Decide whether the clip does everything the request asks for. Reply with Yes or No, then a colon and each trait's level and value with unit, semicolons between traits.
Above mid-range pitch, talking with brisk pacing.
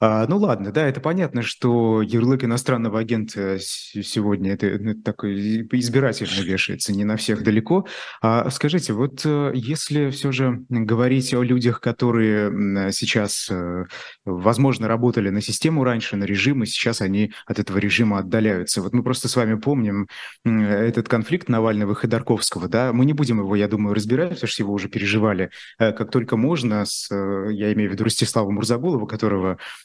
No: low, 115 Hz; fast, 165 wpm